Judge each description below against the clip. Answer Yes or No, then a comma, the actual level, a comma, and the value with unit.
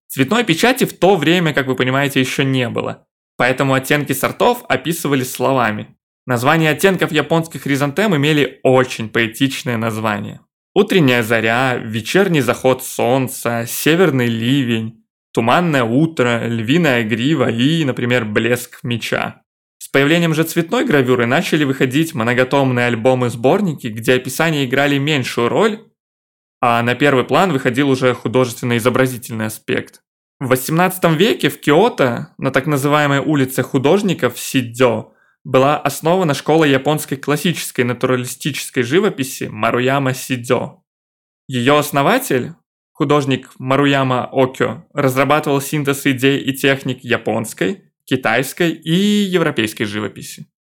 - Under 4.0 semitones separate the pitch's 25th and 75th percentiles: Yes, average, 3.3 semitones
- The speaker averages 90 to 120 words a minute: Yes, average, 115 wpm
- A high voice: No, low, 135 Hz